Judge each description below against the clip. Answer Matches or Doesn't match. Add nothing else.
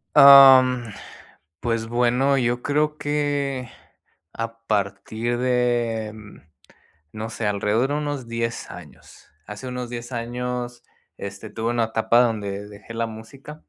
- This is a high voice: Doesn't match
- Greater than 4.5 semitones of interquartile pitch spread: Doesn't match